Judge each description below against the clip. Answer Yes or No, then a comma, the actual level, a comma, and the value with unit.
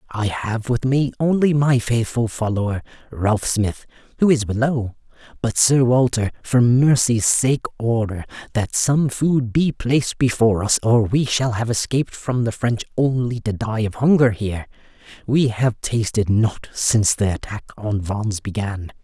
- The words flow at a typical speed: Yes, average, 160 wpm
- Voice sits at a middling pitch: No, low, 120 Hz